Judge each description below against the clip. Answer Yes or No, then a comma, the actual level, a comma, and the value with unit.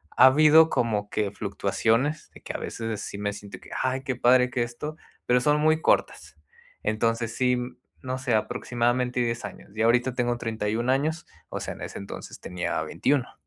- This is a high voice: No, low, 120 Hz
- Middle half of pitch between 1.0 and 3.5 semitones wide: Yes, average, 2.9 semitones